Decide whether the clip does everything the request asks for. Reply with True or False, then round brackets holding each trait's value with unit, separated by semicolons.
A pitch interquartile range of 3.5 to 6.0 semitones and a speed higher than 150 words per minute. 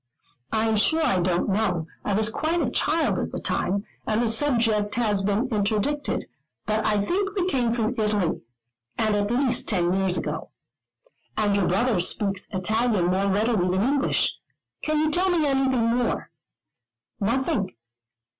True (4.6 semitones; 160 wpm)